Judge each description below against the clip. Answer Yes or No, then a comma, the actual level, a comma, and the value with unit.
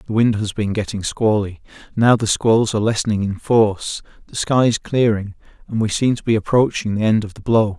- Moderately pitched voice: No, low, 110 Hz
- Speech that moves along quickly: Yes, fast, 215 wpm